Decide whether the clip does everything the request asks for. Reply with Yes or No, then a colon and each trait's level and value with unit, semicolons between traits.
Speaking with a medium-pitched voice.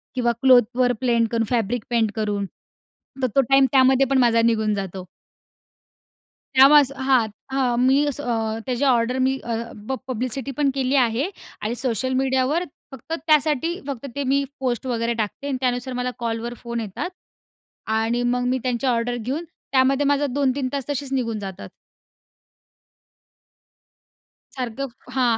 No: very high, 250 Hz